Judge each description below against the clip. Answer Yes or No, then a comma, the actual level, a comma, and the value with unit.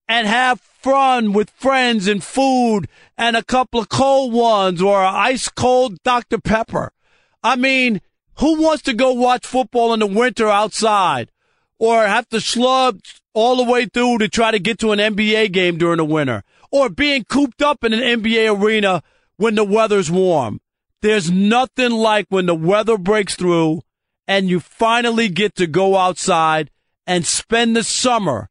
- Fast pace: No, average, 170 wpm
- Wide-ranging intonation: No, average, 4.2 semitones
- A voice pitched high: Yes, high, 225 Hz